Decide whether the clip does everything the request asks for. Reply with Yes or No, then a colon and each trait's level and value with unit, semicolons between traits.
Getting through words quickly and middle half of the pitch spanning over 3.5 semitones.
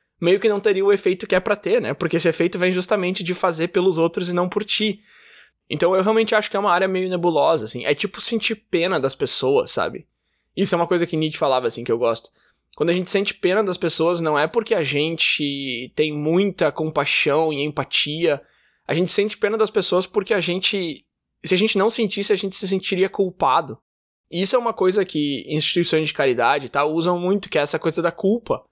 Yes: fast, 225 wpm; average, 4.2 semitones